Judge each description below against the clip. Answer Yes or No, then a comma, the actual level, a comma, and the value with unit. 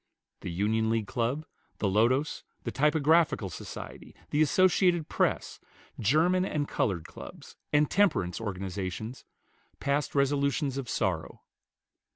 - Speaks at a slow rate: Yes, slow, 115 wpm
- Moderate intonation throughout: No, wide, 6.5 semitones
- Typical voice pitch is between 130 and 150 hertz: Yes, low, 135 Hz